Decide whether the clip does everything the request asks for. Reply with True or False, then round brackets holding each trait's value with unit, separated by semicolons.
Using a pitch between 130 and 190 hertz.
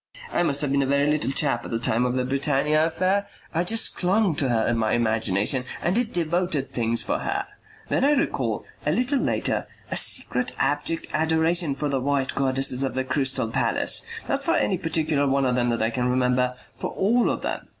True (140 Hz)